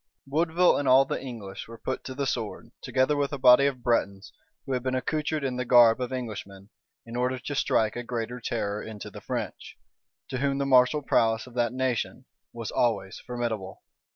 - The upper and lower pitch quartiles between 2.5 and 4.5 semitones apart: Yes, average, 2.8 semitones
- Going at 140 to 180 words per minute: No, average, 195 wpm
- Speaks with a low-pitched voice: Yes, low, 125 Hz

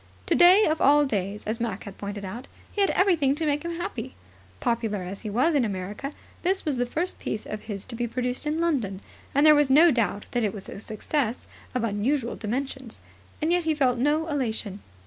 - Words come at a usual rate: No, fast, 210 wpm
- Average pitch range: No, wide, 6.0 semitones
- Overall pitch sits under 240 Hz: No, very high, 250 Hz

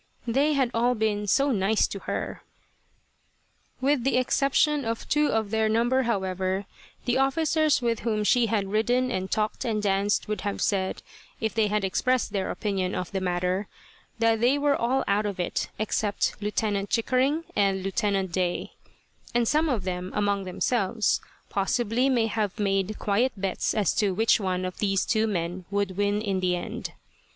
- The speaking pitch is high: Yes, high, 210 Hz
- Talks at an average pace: Yes, average, 170 wpm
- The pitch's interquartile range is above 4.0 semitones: No, average, 3.6 semitones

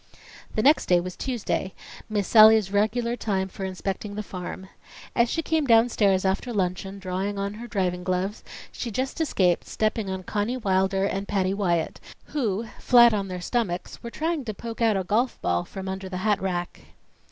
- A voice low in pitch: No, high, 200 Hz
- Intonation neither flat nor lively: Yes, average, 3.4 semitones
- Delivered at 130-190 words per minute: Yes, average, 180 wpm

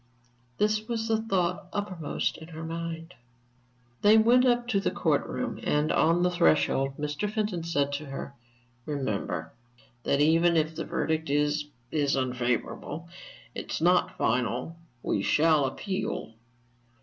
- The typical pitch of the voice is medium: Yes, medium, 160 Hz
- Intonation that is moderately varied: Yes, average, 4.7 semitones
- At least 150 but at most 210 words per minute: No, average, 140 wpm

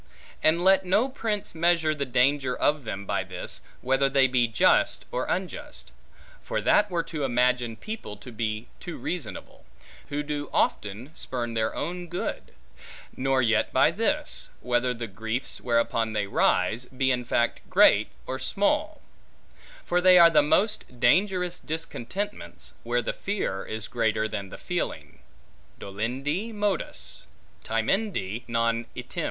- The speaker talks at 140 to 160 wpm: Yes, average, 145 wpm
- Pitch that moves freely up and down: Yes, wide, 7.3 semitones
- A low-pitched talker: Yes, low, 130 Hz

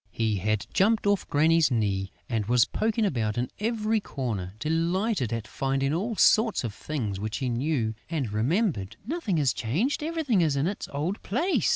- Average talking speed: Yes, average, 175 wpm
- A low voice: No, medium, 145 Hz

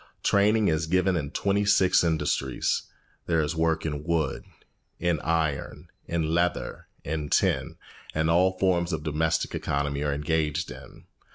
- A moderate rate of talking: Yes, average, 145 wpm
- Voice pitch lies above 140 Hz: No, very low, 80 Hz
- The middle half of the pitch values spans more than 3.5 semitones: No, narrow, 2.5 semitones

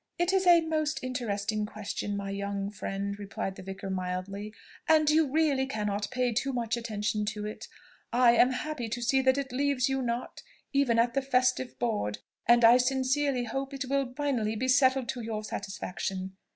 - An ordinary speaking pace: Yes, average, 180 wpm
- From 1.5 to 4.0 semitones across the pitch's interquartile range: No, average, 4.4 semitones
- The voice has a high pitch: Yes, high, 240 Hz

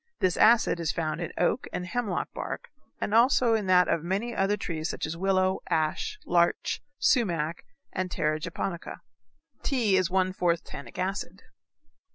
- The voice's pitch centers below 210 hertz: Yes, medium, 185 Hz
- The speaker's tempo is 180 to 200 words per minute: No, average, 160 wpm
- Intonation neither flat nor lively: Yes, average, 3.5 semitones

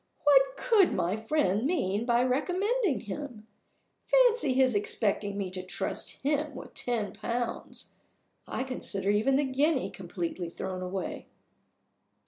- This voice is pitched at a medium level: No, high, 245 Hz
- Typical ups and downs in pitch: No, wide, 6.7 semitones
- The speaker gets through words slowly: Yes, slow, 125 wpm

